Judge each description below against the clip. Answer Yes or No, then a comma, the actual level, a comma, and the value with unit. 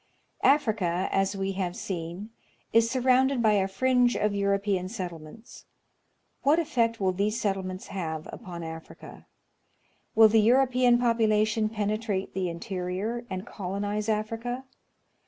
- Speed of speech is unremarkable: No, slow, 125 wpm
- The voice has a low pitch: No, high, 210 Hz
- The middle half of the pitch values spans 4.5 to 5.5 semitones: No, average, 3.6 semitones